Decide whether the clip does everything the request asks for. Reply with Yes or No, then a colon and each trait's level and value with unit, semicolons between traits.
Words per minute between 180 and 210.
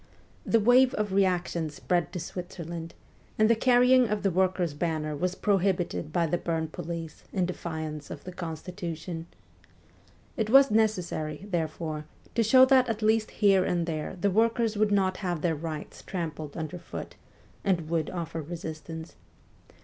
No: average, 150 wpm